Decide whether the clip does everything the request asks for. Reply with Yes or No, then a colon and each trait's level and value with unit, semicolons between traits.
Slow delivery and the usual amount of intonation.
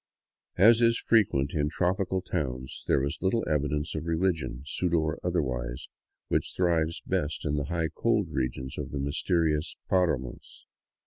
No: average, 145 wpm; average, 4.2 semitones